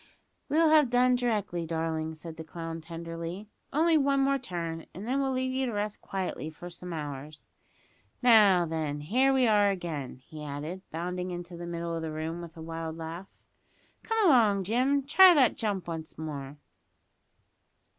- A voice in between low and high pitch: Yes, medium, 175 Hz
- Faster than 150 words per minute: Yes, average, 170 wpm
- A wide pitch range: Yes, wide, 7.2 semitones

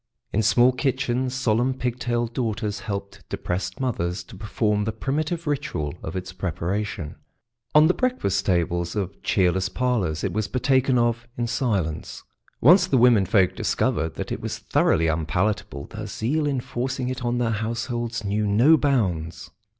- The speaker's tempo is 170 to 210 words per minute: No, average, 155 wpm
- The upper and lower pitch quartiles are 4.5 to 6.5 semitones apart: Yes, average, 5.1 semitones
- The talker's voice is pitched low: Yes, low, 110 Hz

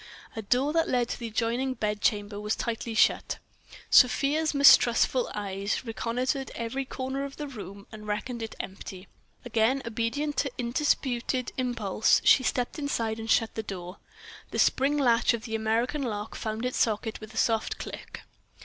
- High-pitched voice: Yes, high, 235 Hz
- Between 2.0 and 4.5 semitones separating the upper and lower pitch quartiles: Yes, average, 3.2 semitones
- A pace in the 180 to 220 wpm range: No, average, 160 wpm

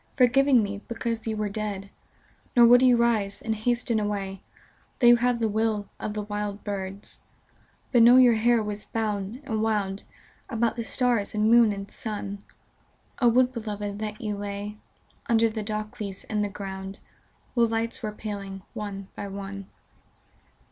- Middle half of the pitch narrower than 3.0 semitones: Yes, narrow, 2.5 semitones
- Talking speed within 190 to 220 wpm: No, average, 165 wpm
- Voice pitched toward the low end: No, high, 215 Hz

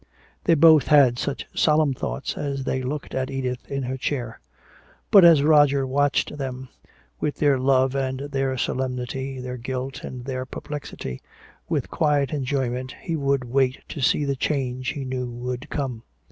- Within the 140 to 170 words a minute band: Yes, average, 160 wpm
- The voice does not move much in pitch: Yes, narrow, 1.9 semitones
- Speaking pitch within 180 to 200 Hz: No, low, 135 Hz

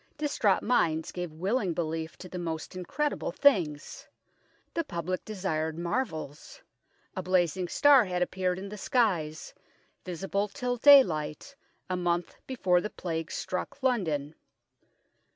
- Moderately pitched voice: Yes, medium, 180 Hz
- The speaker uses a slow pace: Yes, slow, 130 wpm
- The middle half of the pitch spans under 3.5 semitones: No, average, 4.9 semitones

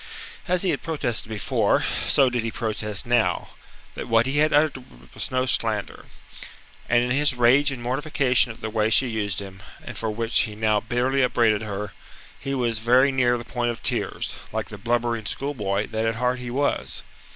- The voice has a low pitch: Yes, low, 120 Hz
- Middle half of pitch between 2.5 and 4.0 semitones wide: Yes, average, 2.9 semitones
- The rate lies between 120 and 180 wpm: No, average, 190 wpm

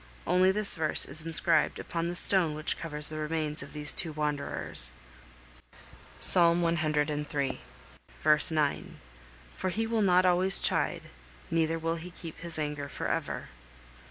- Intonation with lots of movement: No, narrow, 2.6 semitones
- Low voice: No, medium, 160 Hz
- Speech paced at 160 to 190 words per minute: No, average, 145 wpm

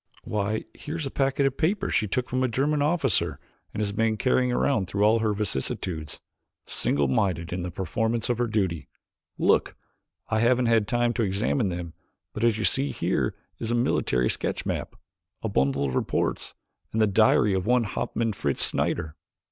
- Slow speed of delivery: No, average, 185 wpm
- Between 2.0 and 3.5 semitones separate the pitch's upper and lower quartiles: No, average, 4.5 semitones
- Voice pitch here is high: No, low, 110 Hz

